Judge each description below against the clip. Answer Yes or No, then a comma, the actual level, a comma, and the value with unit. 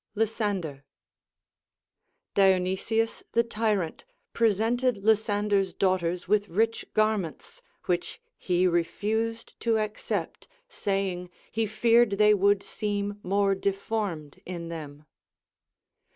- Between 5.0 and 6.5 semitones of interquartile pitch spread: No, average, 3.2 semitones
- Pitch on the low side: No, high, 205 Hz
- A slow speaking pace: Yes, slow, 95 wpm